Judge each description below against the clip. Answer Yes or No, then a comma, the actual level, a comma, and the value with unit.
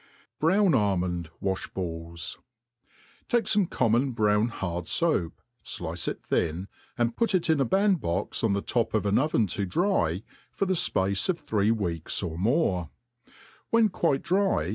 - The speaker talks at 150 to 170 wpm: Yes, average, 155 wpm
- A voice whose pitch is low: Yes, low, 110 Hz